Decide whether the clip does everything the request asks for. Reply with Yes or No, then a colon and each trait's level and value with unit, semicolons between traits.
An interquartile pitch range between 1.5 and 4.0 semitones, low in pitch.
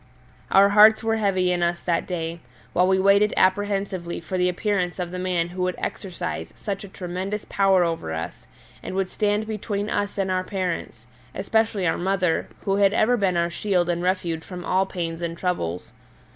No: narrow, 2.4 semitones; medium, 185 Hz